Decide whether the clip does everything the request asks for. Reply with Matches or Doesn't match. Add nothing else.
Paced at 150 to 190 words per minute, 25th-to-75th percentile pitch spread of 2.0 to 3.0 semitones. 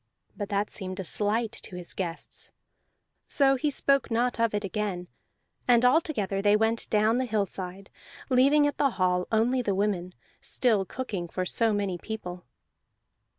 Doesn't match